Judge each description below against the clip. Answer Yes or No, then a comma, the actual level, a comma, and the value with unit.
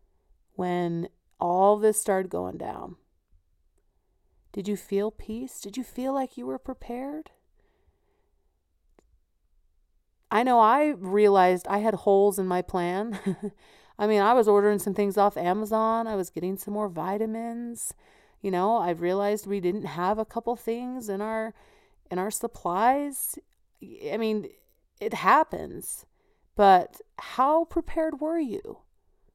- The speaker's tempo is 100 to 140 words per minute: Yes, slow, 135 wpm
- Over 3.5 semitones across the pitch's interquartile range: Yes, average, 4.1 semitones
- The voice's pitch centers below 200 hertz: No, high, 210 Hz